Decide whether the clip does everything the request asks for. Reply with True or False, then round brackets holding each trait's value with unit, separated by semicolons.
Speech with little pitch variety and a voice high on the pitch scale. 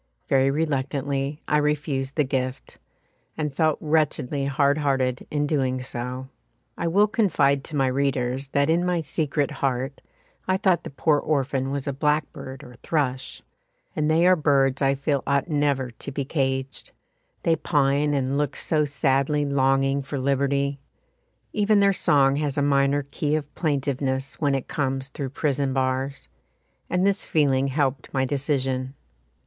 False (1.9 semitones; 140 Hz)